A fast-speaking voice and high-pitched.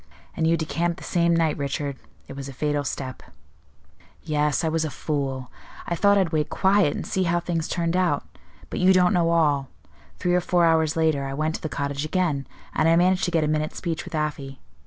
No: fast, 220 wpm; medium, 160 Hz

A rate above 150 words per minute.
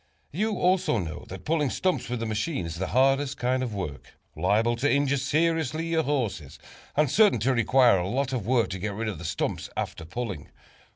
Yes: fast, 205 wpm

